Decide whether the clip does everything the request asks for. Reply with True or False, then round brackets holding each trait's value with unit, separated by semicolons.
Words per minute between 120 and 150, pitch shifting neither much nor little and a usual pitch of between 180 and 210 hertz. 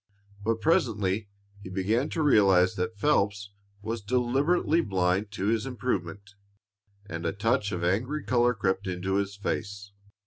False (140 wpm; 4.0 semitones; 105 Hz)